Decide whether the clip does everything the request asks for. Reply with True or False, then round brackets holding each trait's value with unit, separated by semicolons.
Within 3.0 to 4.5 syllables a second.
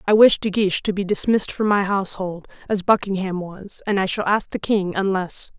False (5.5 syllables/s)